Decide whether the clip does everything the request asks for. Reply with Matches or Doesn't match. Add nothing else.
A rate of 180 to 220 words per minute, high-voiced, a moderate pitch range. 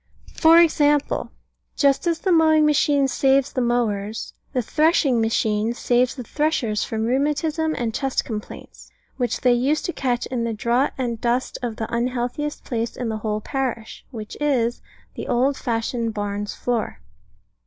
Doesn't match